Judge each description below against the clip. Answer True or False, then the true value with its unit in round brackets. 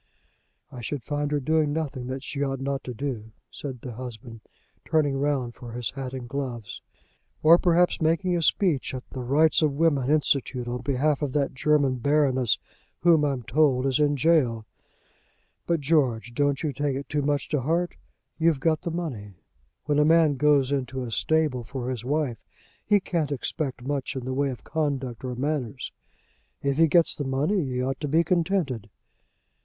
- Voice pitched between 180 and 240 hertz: False (140 Hz)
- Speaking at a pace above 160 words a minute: True (180 wpm)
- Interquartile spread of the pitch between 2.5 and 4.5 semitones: True (3.2 semitones)